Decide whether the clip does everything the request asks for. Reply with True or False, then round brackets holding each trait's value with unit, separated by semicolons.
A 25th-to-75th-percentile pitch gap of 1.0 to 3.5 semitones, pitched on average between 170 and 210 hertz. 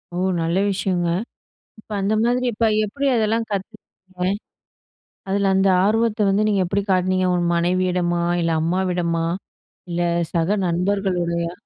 True (2.7 semitones; 185 Hz)